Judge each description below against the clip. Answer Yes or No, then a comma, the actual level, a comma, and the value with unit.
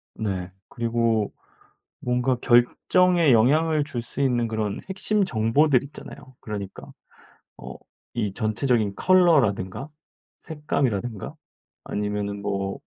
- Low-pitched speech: Yes, low, 120 Hz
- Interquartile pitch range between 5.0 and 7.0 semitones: Yes, wide, 5.6 semitones